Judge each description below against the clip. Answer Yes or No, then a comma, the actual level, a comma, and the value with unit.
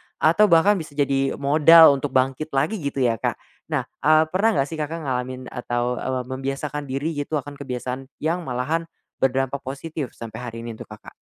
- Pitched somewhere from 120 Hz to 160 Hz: Yes, medium, 140 Hz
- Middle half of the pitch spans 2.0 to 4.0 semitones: Yes, average, 3.3 semitones